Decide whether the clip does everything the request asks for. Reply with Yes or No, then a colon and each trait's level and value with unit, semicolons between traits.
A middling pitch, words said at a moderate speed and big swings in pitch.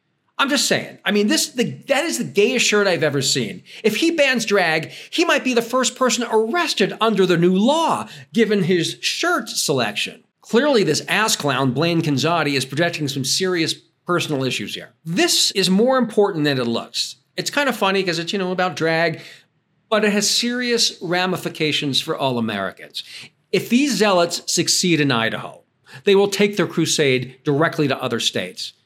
Yes: medium, 180 Hz; average, 180 wpm; wide, 6.4 semitones